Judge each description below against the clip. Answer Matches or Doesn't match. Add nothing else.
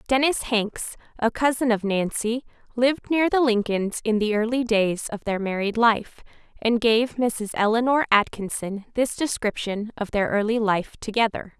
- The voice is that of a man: Doesn't match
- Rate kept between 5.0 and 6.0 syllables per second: Doesn't match